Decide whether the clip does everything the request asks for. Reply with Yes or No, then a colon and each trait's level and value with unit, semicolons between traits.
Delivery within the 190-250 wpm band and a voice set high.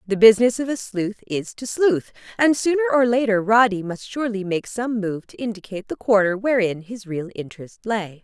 Yes: average, 195 wpm; high, 215 Hz